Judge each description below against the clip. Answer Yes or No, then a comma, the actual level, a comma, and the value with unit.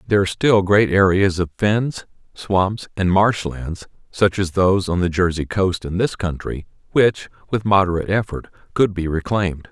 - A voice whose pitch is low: Yes, very low, 95 Hz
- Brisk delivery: No, average, 165 wpm